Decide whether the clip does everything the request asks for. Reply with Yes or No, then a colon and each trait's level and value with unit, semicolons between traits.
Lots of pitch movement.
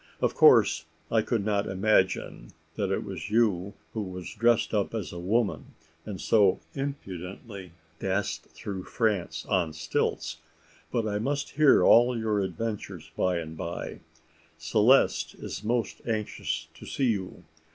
No: average, 3.7 semitones